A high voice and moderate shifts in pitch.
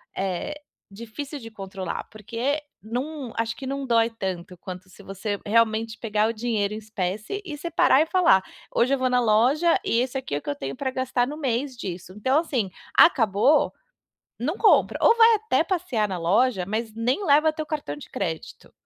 No: high, 230 Hz; wide, 5.7 semitones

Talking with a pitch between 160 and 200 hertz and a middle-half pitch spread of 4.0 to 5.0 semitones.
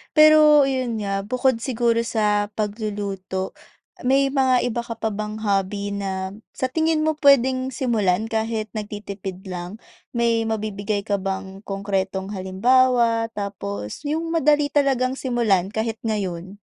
No: high, 220 Hz; average, 4.5 semitones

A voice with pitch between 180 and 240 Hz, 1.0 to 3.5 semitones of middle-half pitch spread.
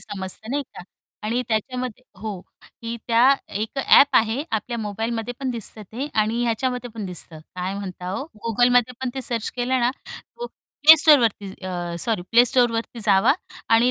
Yes: high, 230 Hz; average, 3.0 semitones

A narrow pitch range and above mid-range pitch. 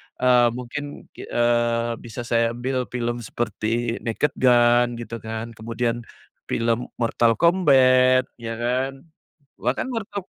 No: narrow, 1.6 semitones; low, 120 Hz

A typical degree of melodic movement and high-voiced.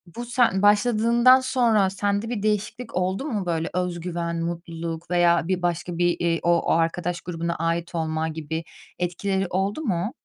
No: average, 3.6 semitones; medium, 180 Hz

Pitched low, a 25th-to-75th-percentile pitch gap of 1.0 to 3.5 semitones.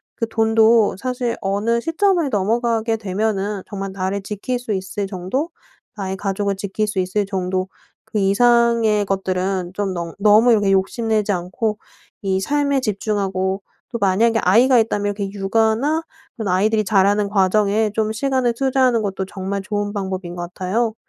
No: high, 205 Hz; average, 2.8 semitones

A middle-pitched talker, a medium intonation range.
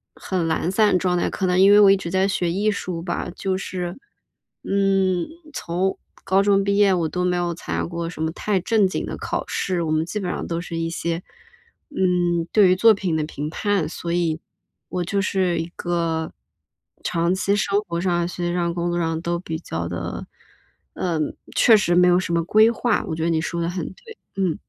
No: medium, 175 Hz; narrow, 2.3 semitones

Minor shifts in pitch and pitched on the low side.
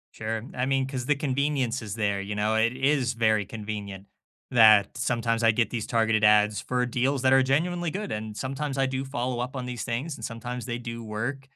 No: average, 3.4 semitones; low, 120 Hz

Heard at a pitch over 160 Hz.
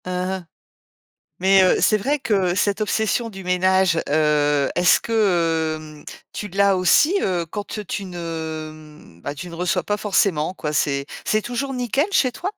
Yes: medium, 185 Hz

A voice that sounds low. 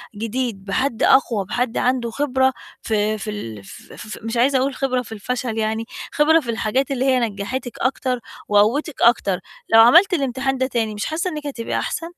No: high, 245 Hz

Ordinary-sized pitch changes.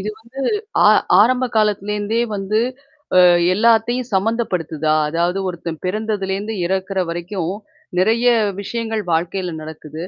Yes: average, 4.1 semitones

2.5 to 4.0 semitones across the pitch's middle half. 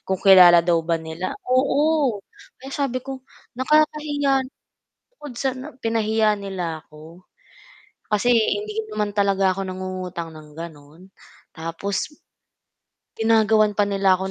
No: wide, 5.5 semitones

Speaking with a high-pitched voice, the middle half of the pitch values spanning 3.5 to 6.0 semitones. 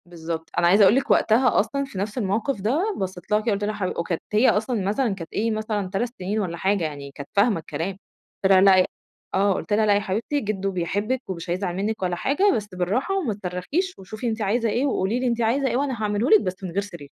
Yes: high, 205 Hz; average, 3.8 semitones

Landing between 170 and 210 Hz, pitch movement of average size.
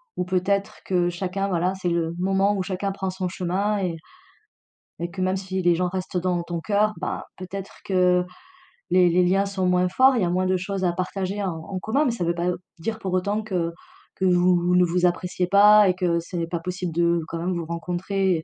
No: medium, 185 Hz; narrow, 1.7 semitones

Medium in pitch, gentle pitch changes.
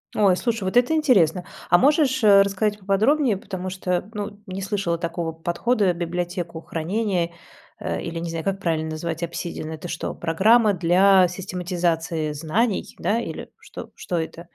No: medium, 180 Hz; average, 3.5 semitones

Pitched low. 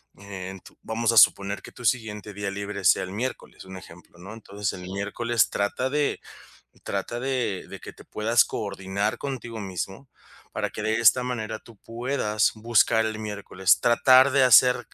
Yes: low, 110 Hz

